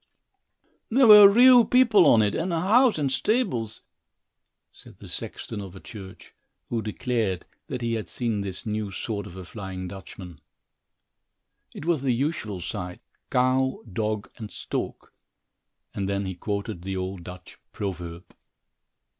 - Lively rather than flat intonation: Yes, wide, 6.4 semitones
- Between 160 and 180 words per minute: No, average, 145 wpm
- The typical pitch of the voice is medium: No, low, 110 Hz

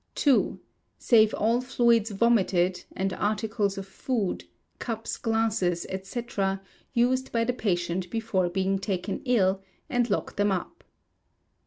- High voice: Yes, high, 210 Hz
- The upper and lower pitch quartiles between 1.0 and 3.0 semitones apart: No, average, 3.6 semitones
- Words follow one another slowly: Yes, slow, 125 wpm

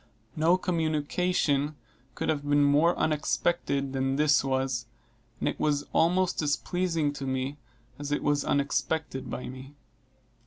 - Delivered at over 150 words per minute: No, average, 140 wpm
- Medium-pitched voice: Yes, medium, 145 Hz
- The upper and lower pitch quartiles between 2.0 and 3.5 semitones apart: Yes, narrow, 2.5 semitones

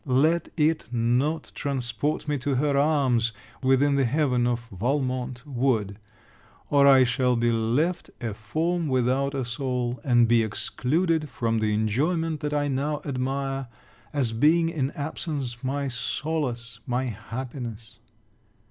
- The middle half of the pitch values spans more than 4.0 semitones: No, average, 3.6 semitones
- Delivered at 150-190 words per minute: No, slow, 135 wpm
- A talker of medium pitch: No, low, 130 Hz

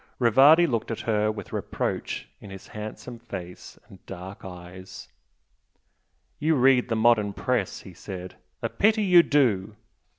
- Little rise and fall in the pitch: No, average, 4.9 semitones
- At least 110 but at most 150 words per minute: Yes, average, 140 wpm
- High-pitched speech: No, low, 110 Hz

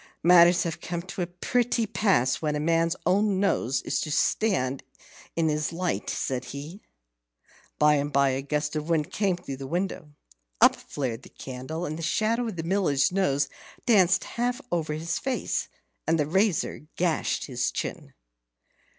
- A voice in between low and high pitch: Yes, medium, 165 Hz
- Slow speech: No, average, 165 wpm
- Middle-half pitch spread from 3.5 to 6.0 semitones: Yes, average, 4.2 semitones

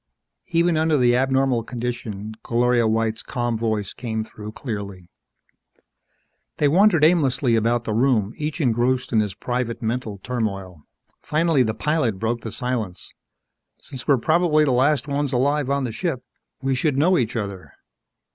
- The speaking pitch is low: Yes, low, 125 Hz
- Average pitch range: Yes, average, 4.2 semitones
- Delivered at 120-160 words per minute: Yes, average, 150 wpm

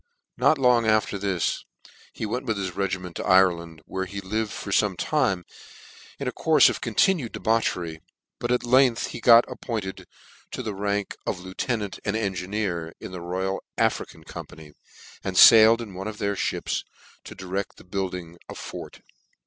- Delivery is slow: No, average, 165 wpm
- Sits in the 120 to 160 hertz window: No, low, 100 Hz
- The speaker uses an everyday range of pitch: Yes, average, 3.4 semitones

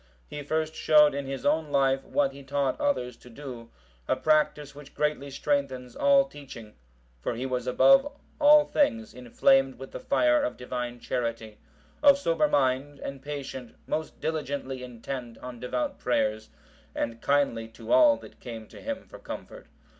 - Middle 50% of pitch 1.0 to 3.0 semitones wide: No, average, 3.7 semitones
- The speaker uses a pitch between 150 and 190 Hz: No, low, 135 Hz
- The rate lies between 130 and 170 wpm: Yes, average, 160 wpm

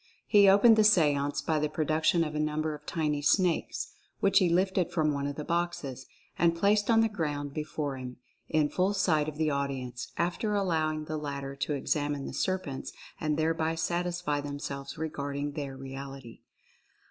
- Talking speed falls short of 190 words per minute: Yes, average, 180 wpm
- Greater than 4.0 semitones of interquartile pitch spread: No, average, 3.4 semitones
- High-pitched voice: No, medium, 155 Hz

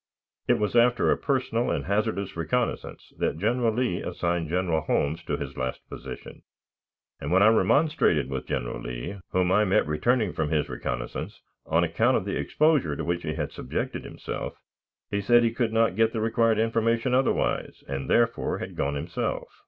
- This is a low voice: Yes, low, 100 Hz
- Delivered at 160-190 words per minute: Yes, average, 175 wpm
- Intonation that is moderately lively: No, wide, 6.6 semitones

